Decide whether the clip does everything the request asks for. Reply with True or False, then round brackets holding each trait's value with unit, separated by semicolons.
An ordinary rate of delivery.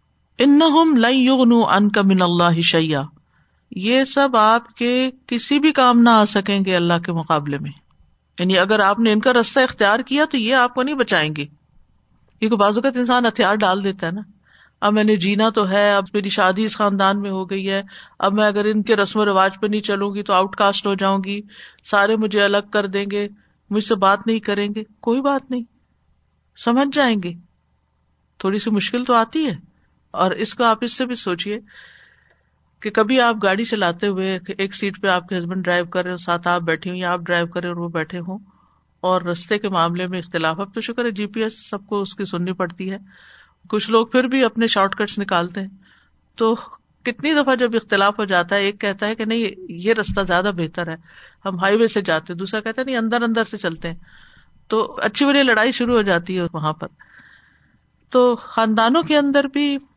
False (210 wpm)